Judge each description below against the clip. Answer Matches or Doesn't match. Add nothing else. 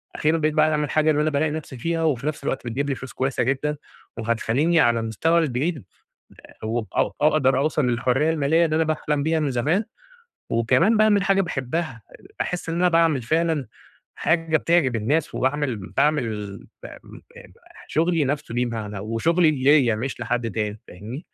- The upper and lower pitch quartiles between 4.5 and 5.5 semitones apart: Matches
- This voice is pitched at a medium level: Matches